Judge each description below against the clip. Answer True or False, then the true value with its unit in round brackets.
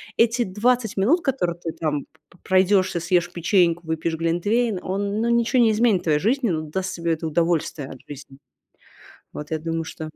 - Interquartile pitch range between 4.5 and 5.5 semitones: True (5.0 semitones)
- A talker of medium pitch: True (180 Hz)